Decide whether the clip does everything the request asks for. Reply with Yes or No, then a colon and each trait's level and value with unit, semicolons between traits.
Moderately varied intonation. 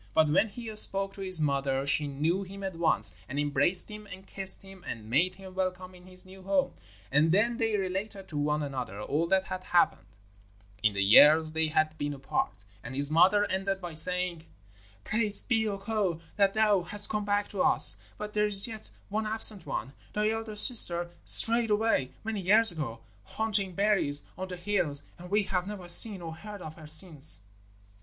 Yes: average, 4.8 semitones